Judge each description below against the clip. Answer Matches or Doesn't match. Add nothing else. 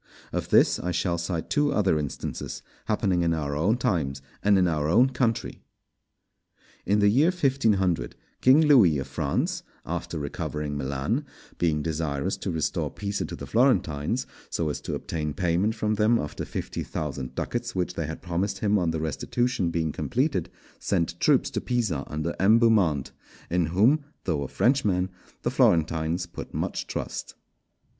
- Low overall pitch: Matches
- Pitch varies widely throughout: Matches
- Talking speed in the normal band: Matches